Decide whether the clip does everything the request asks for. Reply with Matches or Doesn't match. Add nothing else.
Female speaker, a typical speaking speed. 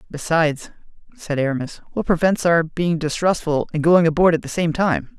Doesn't match